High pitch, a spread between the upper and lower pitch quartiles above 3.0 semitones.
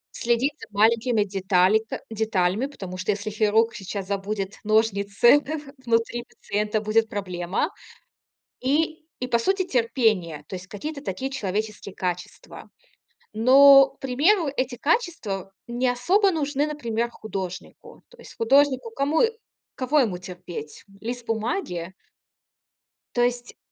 Yes: high, 225 Hz; average, 5.0 semitones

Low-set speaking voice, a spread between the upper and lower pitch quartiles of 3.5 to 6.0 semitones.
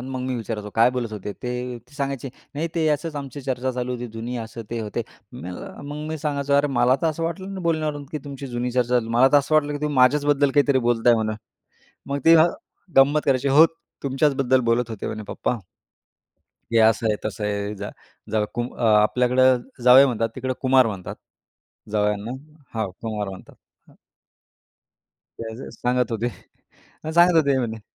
Yes: low, 125 Hz; average, 3.9 semitones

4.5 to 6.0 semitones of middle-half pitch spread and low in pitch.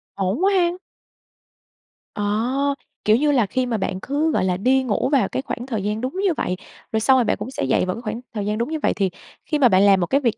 No: average, 4.8 semitones; high, 235 Hz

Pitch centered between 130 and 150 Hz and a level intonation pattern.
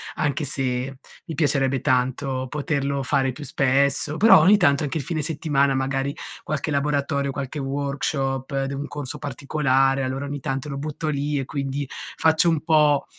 Yes: medium, 140 Hz; narrow, 1.8 semitones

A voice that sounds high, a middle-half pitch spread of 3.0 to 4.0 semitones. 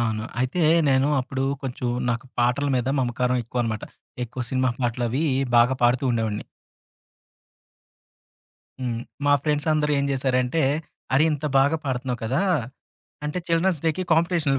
No: low, 130 Hz; average, 3.4 semitones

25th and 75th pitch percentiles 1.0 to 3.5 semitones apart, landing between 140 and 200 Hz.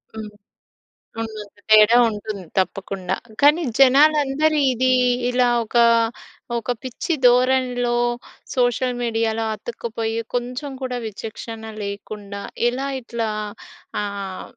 No: average, 2.9 semitones; high, 235 Hz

